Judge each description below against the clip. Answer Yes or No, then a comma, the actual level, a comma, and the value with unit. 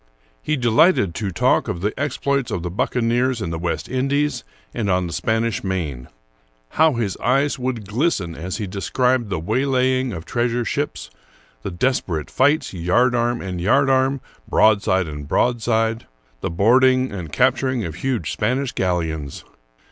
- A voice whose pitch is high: No, low, 115 Hz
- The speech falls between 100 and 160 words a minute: Yes, average, 155 wpm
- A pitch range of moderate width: No, wide, 6.0 semitones